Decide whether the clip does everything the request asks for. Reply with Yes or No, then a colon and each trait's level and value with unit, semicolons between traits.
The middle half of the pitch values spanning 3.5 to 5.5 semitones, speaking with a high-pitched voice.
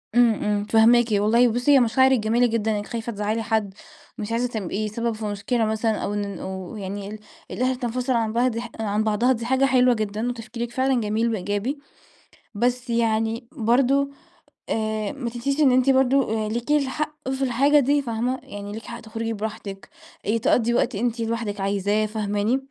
No: narrow, 2.6 semitones; high, 230 Hz